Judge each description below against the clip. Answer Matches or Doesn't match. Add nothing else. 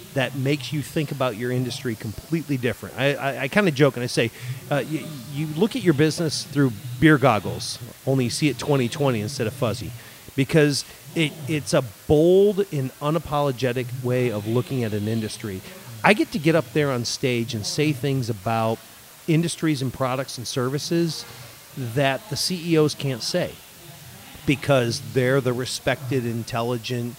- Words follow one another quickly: Doesn't match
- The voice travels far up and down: Doesn't match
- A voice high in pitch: Doesn't match